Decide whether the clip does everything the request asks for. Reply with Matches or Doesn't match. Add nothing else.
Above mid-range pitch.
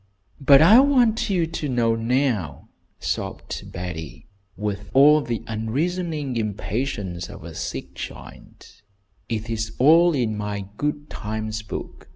Doesn't match